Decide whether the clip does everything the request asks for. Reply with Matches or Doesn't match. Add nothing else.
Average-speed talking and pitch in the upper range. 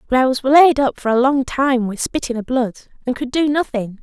Doesn't match